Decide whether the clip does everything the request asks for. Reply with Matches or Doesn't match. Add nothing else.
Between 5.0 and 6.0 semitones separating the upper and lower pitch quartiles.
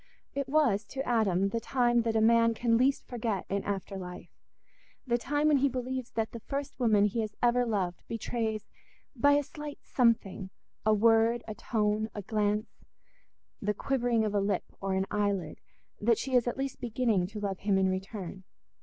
Doesn't match